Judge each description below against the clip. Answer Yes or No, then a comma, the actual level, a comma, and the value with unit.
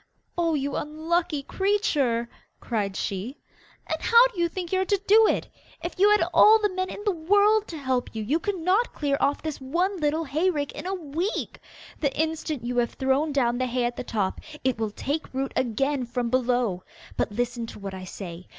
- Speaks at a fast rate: Yes, fast, 210 wpm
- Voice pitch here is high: Yes, very high, 290 Hz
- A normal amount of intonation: No, wide, 6.9 semitones